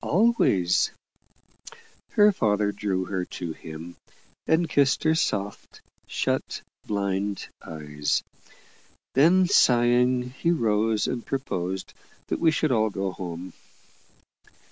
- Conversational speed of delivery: No, slow, 105 wpm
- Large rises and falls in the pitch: Yes, wide, 6.8 semitones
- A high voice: No, low, 105 Hz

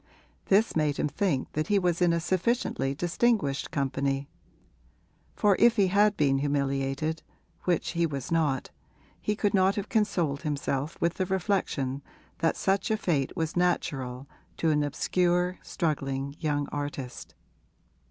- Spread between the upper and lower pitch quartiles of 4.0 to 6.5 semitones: Yes, average, 5.1 semitones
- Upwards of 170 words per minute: No, average, 140 wpm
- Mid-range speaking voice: Yes, medium, 160 Hz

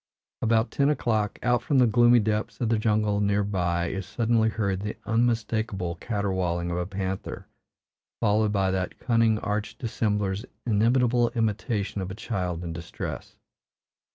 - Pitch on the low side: Yes, low, 105 Hz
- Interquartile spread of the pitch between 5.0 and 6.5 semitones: No, average, 3.1 semitones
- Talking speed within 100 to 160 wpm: Yes, average, 150 wpm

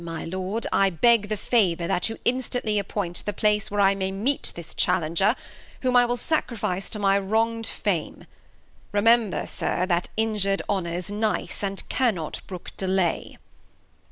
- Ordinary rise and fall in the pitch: Yes, average, 3.4 semitones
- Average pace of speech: Yes, average, 155 wpm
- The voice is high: Yes, high, 200 Hz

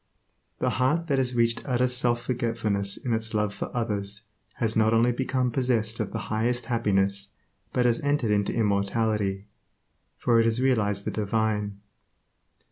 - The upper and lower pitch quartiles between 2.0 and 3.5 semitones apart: Yes, average, 2.9 semitones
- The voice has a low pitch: Yes, low, 115 Hz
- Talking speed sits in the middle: Yes, average, 155 wpm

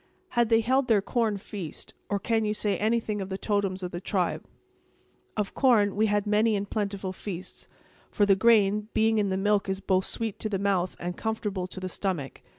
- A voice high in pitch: Yes, high, 205 Hz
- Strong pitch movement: No, narrow, 2.4 semitones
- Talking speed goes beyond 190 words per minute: Yes, average, 200 wpm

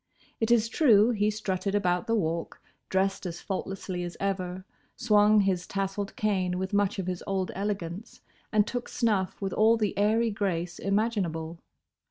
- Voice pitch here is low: No, high, 195 Hz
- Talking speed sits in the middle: Yes, average, 160 wpm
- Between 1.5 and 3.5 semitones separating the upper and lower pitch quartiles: Yes, average, 2.7 semitones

